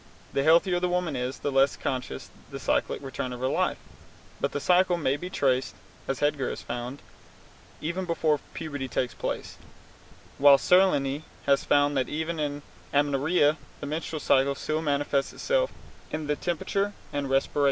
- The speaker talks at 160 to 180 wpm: Yes, average, 165 wpm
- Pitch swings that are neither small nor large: Yes, average, 3.2 semitones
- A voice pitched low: No, medium, 145 Hz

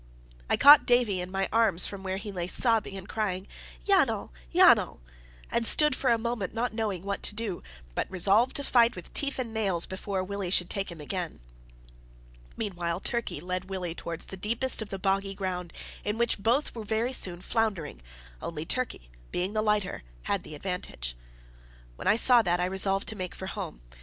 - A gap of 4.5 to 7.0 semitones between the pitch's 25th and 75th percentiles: No, average, 3.7 semitones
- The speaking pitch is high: Yes, high, 195 Hz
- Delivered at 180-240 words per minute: Yes, average, 185 wpm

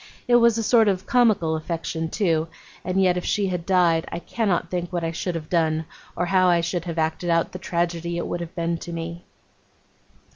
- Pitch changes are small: Yes, narrow, 1.8 semitones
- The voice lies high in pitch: No, medium, 175 Hz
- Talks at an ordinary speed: No, fast, 215 wpm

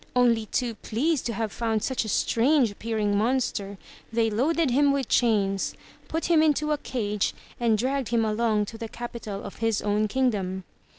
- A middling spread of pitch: Yes, average, 3.6 semitones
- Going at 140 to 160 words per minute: No, average, 175 wpm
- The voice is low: No, high, 230 Hz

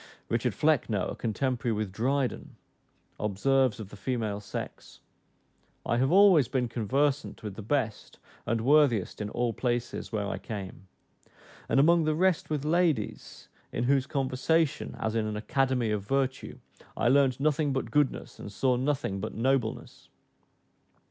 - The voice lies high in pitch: No, low, 125 Hz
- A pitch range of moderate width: Yes, average, 4.3 semitones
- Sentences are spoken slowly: No, average, 150 wpm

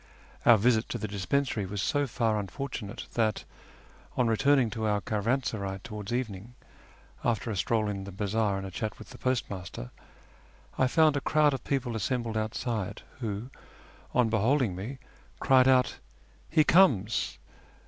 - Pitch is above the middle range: No, low, 115 Hz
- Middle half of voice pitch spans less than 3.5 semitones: No, average, 3.9 semitones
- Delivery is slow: No, average, 155 wpm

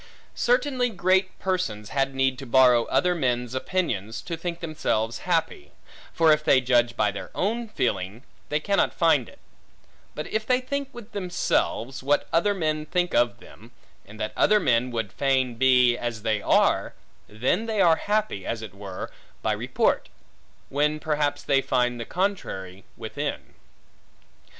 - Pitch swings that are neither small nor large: No, wide, 7.6 semitones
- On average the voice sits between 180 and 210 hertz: No, low, 135 Hz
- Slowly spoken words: No, average, 155 wpm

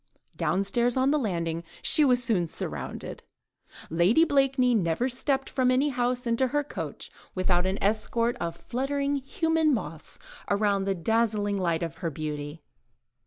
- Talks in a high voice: Yes, high, 230 Hz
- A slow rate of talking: No, average, 145 wpm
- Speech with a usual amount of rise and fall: No, wide, 6.7 semitones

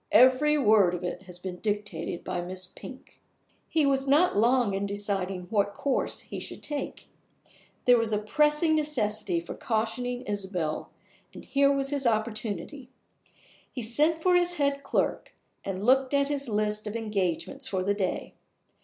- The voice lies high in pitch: Yes, high, 225 Hz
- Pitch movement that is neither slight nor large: No, wide, 5.7 semitones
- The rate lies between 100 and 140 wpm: No, average, 160 wpm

